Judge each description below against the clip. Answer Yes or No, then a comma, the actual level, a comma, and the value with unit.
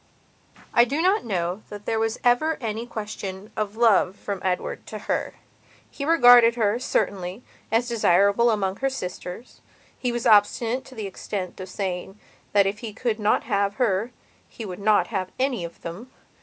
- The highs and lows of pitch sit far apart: No, average, 3.6 semitones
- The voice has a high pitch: Yes, high, 215 Hz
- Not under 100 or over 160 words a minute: No, average, 170 wpm